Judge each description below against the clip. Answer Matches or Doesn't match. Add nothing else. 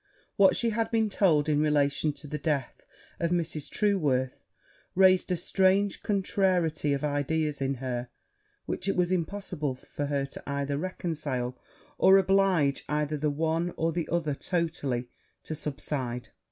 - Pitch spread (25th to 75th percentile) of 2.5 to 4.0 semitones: Doesn't match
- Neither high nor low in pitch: Matches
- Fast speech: Doesn't match